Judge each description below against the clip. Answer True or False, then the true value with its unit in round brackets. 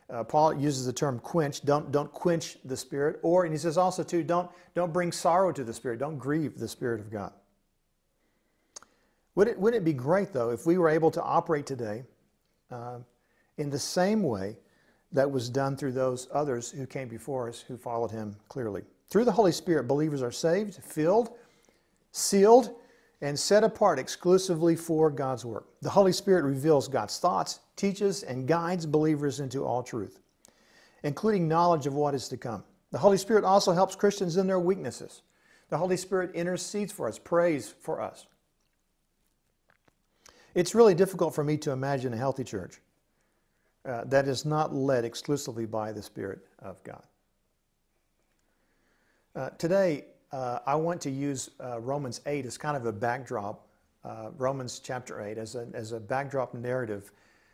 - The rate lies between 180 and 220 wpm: False (170 wpm)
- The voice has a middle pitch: True (145 Hz)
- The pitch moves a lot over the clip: True (5.7 semitones)